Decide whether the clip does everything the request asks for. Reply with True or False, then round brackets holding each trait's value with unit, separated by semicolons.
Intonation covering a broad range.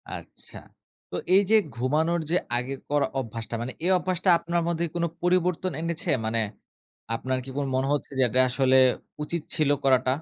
False (4.9 semitones)